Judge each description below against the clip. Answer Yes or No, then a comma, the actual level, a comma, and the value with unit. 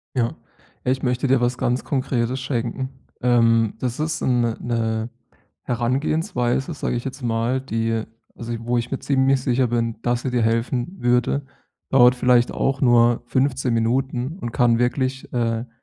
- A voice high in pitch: No, low, 125 Hz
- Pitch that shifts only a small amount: Yes, narrow, 2.0 semitones